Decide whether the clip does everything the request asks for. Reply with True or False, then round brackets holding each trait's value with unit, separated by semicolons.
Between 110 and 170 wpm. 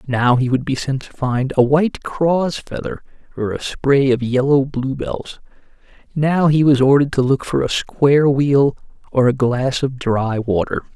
False (180 wpm)